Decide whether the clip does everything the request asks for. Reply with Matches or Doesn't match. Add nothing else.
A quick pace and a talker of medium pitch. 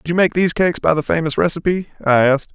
Matches